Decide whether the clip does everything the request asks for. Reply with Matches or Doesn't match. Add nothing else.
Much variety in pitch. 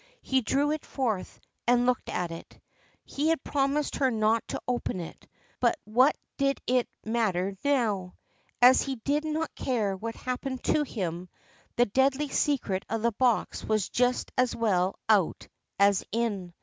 Doesn't match